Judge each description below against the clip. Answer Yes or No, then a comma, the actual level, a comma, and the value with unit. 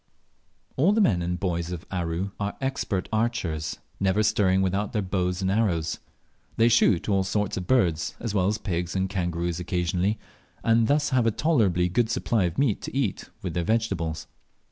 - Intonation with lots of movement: No, average, 4.3 semitones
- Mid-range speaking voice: No, very low, 95 Hz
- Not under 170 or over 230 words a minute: Yes, average, 180 wpm